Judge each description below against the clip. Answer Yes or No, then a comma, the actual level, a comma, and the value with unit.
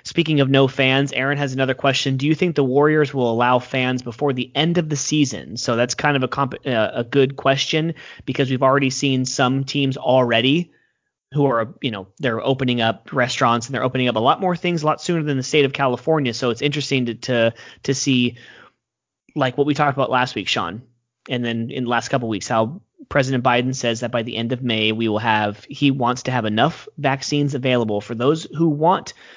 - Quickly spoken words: Yes, fast, 225 wpm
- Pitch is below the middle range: Yes, low, 130 Hz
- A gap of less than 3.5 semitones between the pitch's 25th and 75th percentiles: Yes, average, 2.9 semitones